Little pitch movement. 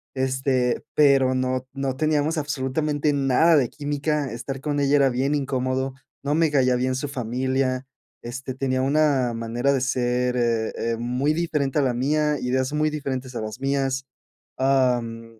Yes: narrow, 2.3 semitones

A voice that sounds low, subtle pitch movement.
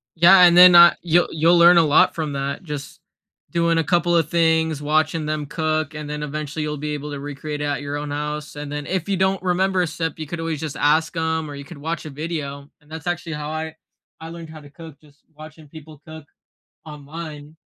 No: medium, 155 Hz; narrow, 2.2 semitones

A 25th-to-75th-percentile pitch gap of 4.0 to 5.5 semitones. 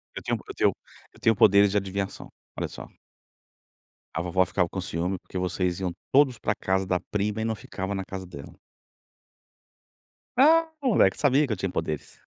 No: average, 3.2 semitones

